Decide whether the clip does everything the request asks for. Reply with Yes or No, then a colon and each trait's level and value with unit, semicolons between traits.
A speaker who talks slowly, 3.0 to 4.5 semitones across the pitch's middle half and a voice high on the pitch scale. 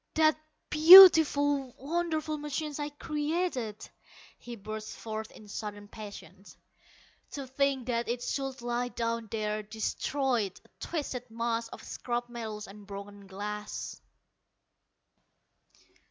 No: slow, 110 wpm; average, 5.3 semitones; high, 240 Hz